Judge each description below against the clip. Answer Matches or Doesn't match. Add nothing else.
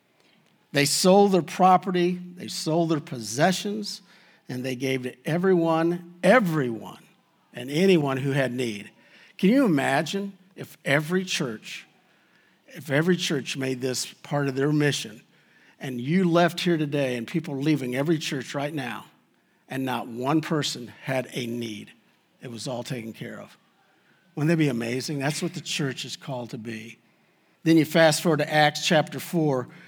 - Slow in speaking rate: Doesn't match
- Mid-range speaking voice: Matches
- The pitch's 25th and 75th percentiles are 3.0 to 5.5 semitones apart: Matches